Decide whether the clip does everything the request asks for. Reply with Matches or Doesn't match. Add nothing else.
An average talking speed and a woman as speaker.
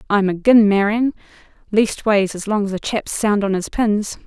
Matches